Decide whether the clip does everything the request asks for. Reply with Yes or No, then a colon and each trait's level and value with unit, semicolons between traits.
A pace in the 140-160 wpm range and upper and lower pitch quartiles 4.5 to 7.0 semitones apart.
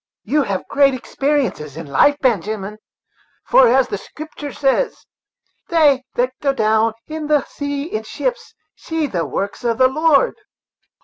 Yes: average, 150 wpm; wide, 5.5 semitones